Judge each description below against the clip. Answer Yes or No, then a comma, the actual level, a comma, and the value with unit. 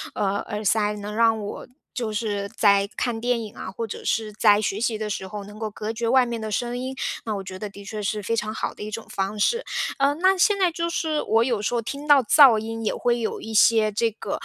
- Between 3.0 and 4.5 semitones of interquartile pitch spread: No, narrow, 2.5 semitones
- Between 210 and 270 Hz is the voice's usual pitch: Yes, high, 220 Hz